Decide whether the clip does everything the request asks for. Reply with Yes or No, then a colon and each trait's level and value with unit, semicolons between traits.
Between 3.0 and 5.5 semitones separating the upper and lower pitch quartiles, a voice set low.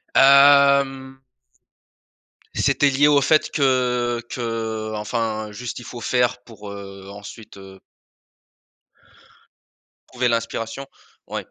Yes: average, 3.7 semitones; low, 120 Hz